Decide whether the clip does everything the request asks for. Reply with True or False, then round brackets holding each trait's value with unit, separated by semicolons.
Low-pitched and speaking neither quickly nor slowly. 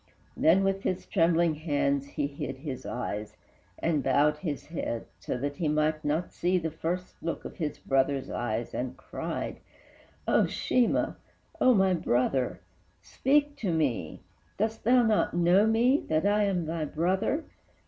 False (160 Hz; 155 wpm)